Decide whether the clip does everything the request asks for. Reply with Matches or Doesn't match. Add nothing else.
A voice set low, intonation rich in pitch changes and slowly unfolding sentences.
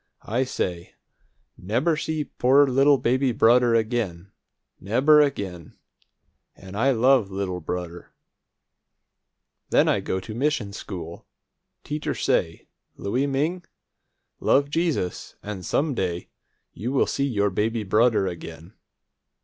Matches